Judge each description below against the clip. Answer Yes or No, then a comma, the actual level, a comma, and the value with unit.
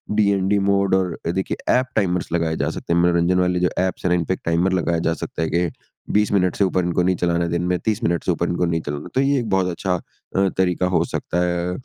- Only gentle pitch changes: Yes, narrow, 1.9 semitones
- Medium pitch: No, very low, 90 Hz